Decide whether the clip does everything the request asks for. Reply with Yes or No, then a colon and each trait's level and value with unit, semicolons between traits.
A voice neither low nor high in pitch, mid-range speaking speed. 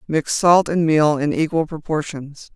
Yes: medium, 155 Hz; average, 165 wpm